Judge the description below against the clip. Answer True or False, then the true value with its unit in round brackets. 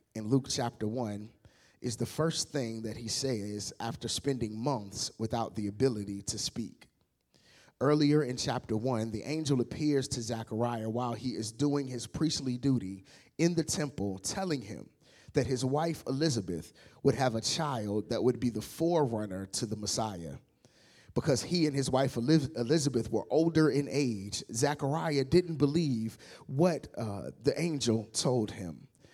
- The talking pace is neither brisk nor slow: True (155 wpm)